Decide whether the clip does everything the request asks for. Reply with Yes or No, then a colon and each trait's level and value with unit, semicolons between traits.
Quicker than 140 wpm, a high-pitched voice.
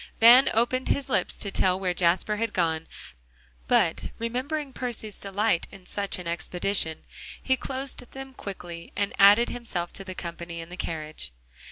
Yes: average, 160 wpm; high, 200 Hz